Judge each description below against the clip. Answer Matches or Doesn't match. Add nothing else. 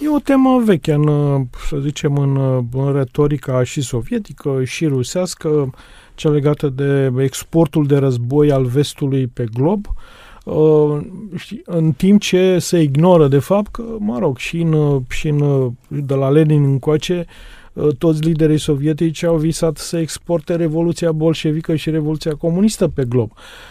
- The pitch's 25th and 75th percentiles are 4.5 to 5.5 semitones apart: Doesn't match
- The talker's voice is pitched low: Doesn't match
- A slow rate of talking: Doesn't match